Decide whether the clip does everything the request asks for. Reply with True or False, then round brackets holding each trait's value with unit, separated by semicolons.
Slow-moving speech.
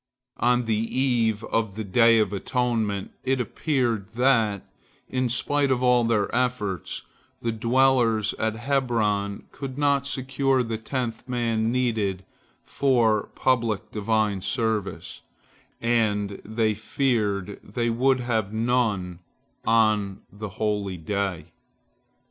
True (115 wpm)